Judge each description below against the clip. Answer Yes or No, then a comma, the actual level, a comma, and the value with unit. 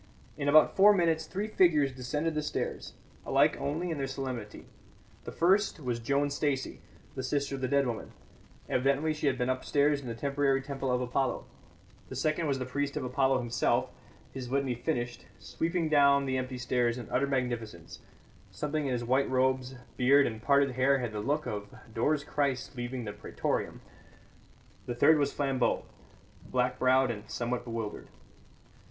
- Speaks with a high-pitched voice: No, low, 135 Hz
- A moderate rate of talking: Yes, average, 170 wpm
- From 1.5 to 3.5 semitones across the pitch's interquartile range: Yes, narrow, 2.5 semitones